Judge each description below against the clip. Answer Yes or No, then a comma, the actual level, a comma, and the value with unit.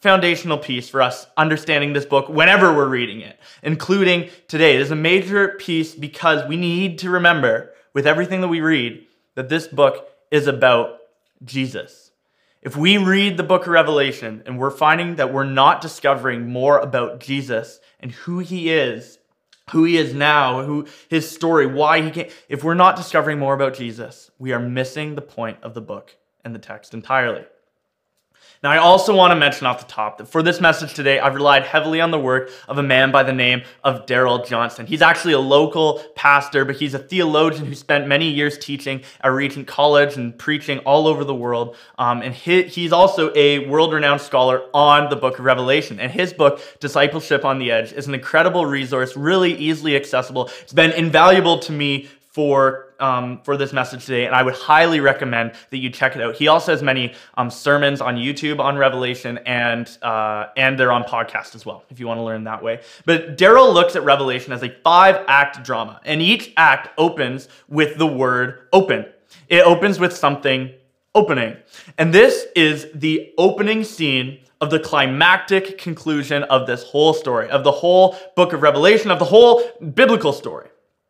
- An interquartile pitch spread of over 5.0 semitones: No, average, 4.0 semitones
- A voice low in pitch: No, medium, 145 Hz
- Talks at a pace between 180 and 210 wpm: Yes, average, 190 wpm